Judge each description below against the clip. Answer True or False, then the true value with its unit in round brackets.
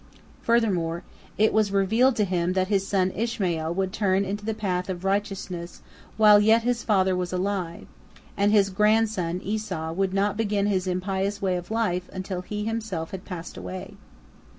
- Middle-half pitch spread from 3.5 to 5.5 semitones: False (2.5 semitones)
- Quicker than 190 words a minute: False (170 wpm)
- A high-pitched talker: True (195 Hz)